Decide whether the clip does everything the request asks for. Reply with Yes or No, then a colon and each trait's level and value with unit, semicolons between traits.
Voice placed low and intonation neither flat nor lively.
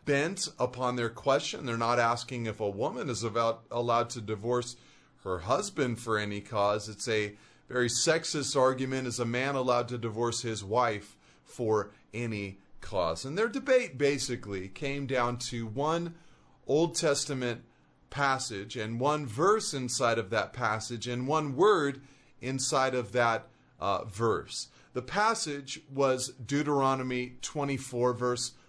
Yes: low, 125 Hz; average, 3.2 semitones